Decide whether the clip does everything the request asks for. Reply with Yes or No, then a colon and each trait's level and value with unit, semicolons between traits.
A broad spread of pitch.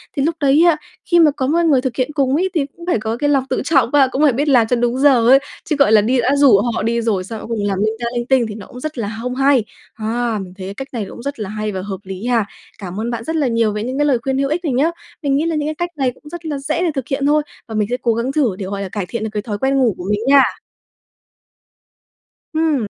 No: average, 4.5 semitones